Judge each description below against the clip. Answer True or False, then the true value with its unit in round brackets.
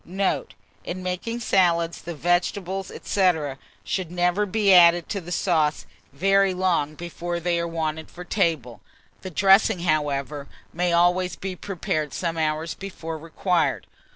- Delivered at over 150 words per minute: False (140 wpm)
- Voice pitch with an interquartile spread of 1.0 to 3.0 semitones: True (2.5 semitones)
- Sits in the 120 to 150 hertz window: False (175 Hz)